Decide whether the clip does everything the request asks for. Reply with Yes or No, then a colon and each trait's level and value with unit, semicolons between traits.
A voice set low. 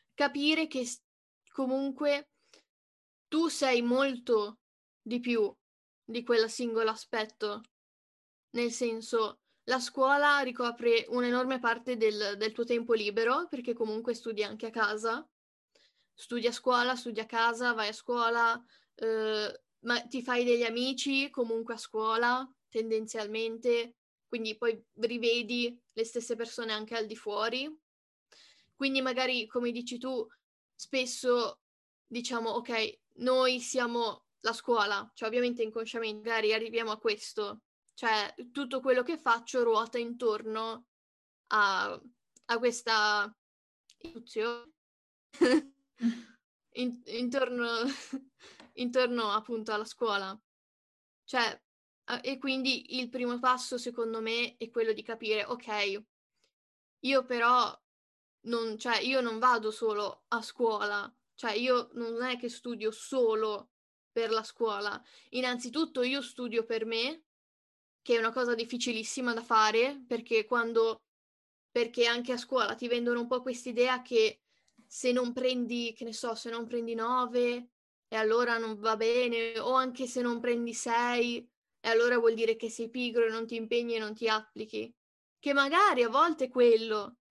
No: high, 235 Hz